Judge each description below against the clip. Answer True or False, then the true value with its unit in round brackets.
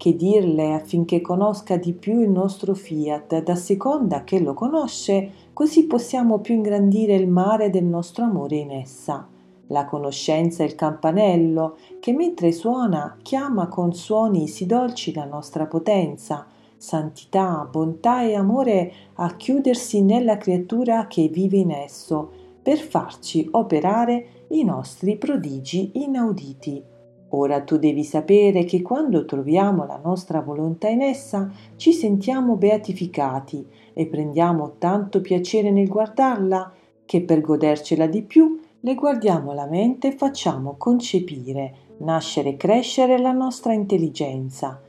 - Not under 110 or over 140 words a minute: True (130 wpm)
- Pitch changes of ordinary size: False (6.0 semitones)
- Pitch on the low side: False (185 Hz)